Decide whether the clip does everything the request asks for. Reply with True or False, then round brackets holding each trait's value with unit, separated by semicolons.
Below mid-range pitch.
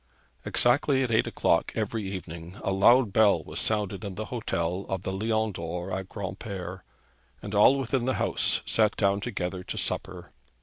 True (100 Hz)